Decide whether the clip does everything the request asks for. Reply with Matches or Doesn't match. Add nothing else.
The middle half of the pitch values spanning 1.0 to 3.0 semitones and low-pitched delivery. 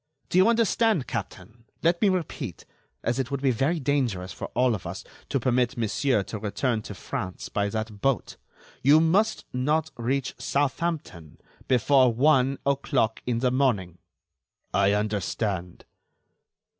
Doesn't match